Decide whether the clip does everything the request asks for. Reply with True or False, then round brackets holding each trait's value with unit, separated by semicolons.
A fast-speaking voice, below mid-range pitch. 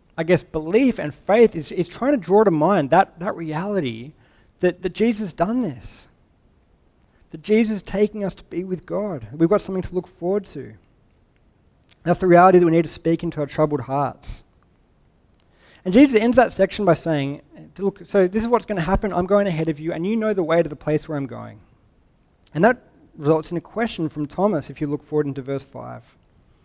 False (215 wpm; 170 Hz)